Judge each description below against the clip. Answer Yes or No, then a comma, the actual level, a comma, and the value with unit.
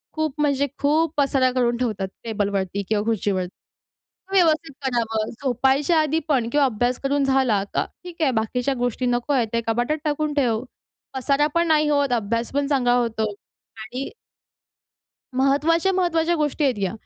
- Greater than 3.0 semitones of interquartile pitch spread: Yes, average, 4.2 semitones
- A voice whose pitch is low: No, very high, 265 Hz